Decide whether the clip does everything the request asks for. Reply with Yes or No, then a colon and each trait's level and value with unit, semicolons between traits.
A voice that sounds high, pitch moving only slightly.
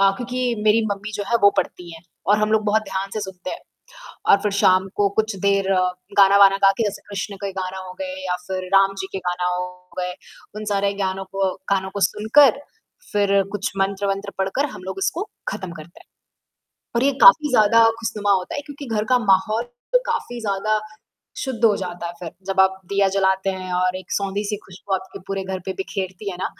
Yes: high, 195 Hz; narrow, 2.0 semitones